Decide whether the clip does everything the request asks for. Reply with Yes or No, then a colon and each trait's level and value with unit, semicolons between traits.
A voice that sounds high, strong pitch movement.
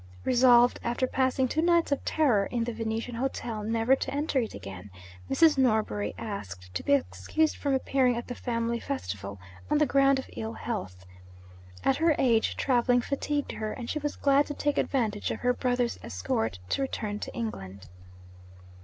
No: high, 245 Hz; average, 4.1 semitones